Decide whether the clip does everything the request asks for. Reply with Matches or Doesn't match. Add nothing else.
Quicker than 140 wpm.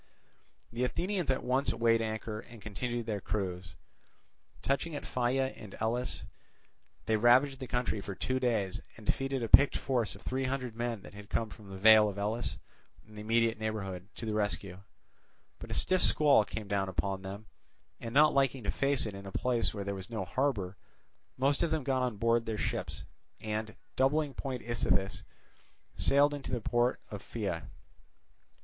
Matches